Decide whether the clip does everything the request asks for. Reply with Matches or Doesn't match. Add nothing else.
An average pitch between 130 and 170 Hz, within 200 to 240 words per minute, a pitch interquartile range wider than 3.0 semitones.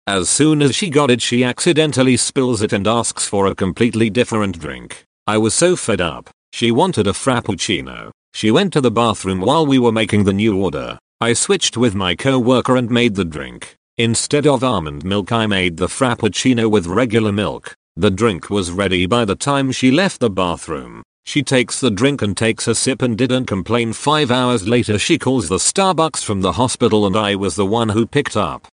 Doesn't match